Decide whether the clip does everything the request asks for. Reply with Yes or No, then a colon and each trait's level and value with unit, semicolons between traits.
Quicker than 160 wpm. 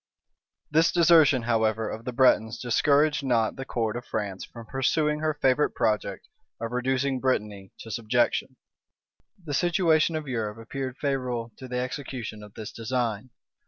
No: average, 150 wpm